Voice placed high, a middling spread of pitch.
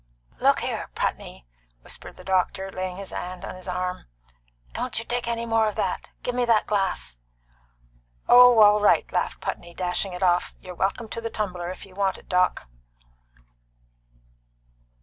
Yes: high, 195 Hz; average, 3.6 semitones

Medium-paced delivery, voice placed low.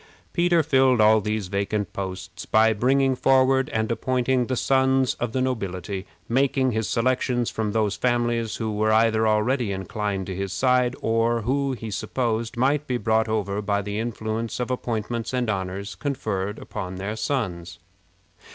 Yes: average, 160 wpm; low, 115 Hz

